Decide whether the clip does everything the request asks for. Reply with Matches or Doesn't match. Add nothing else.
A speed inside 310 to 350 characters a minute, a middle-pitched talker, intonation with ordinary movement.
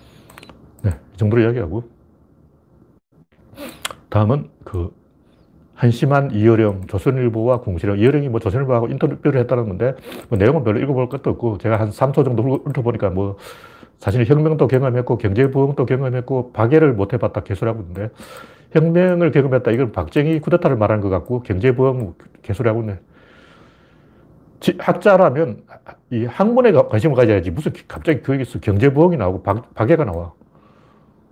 Doesn't match